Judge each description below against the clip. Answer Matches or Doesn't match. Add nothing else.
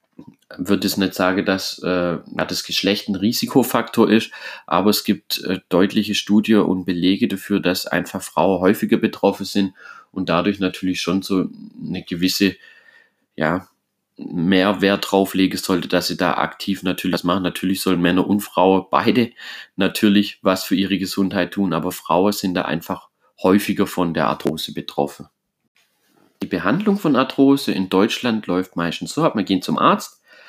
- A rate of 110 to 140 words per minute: Doesn't match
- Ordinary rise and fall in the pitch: Doesn't match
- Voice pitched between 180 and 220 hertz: Doesn't match